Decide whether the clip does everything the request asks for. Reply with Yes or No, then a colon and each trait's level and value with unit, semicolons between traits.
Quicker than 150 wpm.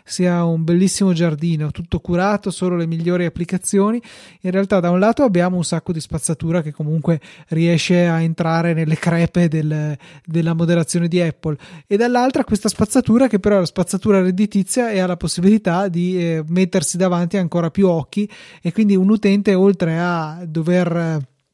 Yes: fast, 170 wpm